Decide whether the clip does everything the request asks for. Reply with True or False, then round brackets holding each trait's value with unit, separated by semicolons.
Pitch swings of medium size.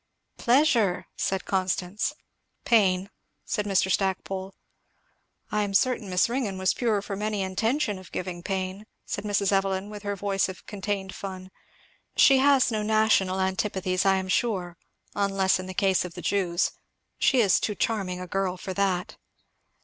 False (2.0 semitones)